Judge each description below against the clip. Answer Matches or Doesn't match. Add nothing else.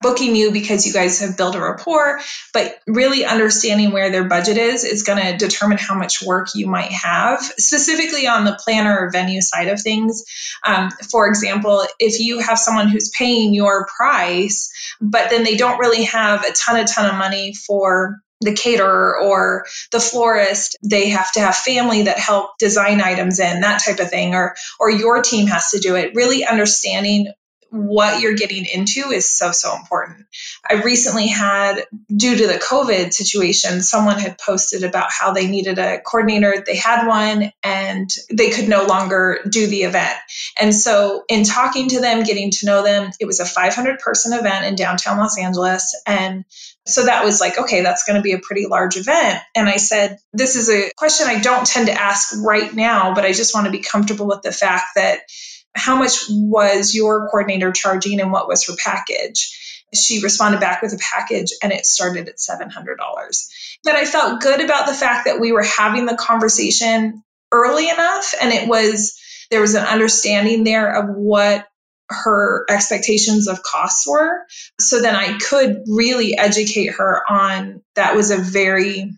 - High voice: Matches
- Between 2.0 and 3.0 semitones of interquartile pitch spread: Matches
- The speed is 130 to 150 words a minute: Doesn't match